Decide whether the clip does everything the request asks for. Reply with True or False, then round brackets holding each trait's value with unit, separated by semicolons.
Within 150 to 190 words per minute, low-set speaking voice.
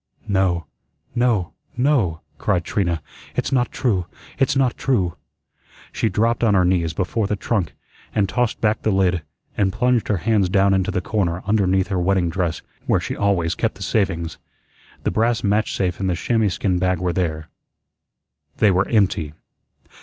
True (170 wpm; 95 Hz)